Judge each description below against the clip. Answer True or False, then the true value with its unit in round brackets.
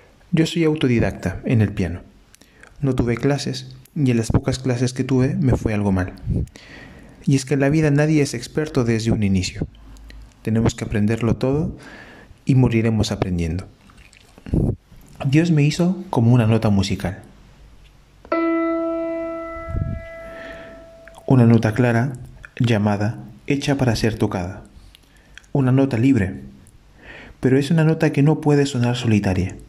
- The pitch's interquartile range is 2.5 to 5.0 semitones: False (5.4 semitones)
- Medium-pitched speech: False (125 Hz)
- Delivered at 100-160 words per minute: True (135 wpm)